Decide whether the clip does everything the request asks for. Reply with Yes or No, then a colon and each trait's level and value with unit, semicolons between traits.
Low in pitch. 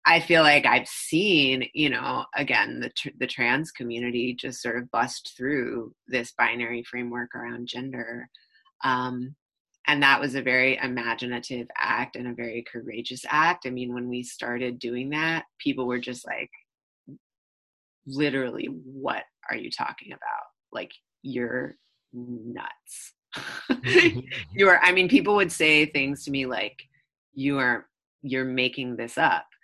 Yes: low, 125 Hz